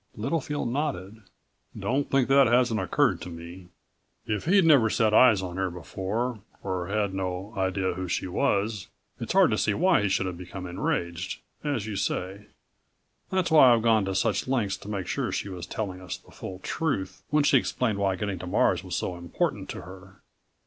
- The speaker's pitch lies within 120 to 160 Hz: No, low, 100 Hz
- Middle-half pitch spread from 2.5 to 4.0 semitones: No, average, 4.5 semitones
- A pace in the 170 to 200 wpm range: Yes, average, 190 wpm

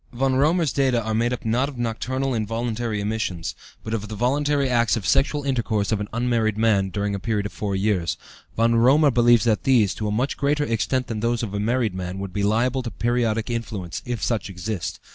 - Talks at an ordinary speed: No, fast, 215 wpm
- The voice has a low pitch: Yes, low, 115 Hz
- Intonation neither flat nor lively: Yes, average, 3.1 semitones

